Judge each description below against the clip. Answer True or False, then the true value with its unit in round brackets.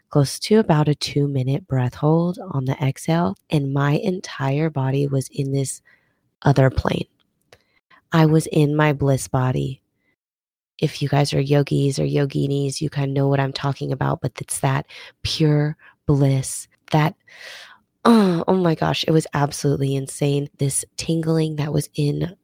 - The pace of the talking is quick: False (160 wpm)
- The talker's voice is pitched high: False (145 Hz)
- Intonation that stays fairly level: True (2.3 semitones)